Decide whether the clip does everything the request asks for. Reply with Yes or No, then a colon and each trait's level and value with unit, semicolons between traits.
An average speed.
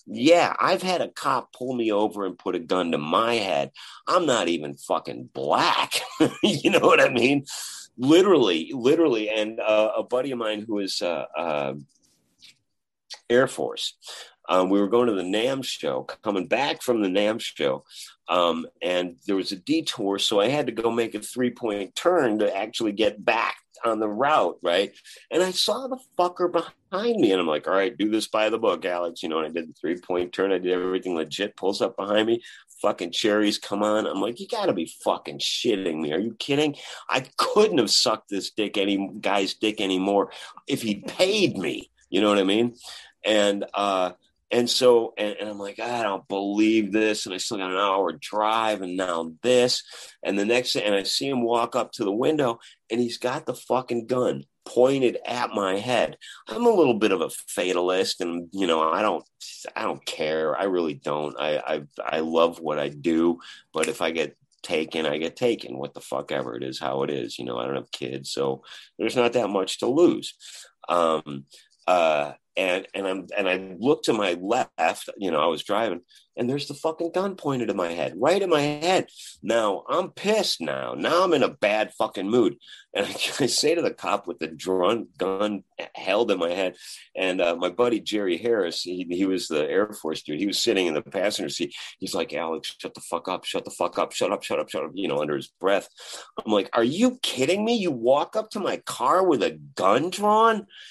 No: fast, 215 wpm